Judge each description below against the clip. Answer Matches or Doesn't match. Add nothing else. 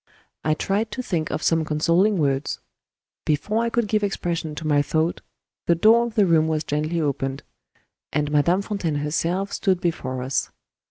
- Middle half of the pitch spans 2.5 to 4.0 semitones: Doesn't match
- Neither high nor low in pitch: Matches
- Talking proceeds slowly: Doesn't match